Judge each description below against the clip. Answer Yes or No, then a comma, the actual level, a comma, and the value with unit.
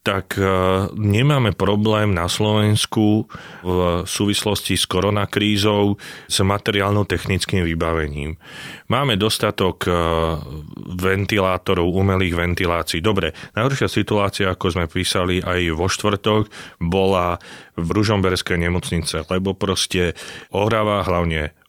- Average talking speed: No, slow, 95 wpm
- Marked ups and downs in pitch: No, average, 2.9 semitones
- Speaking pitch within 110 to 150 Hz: No, very low, 95 Hz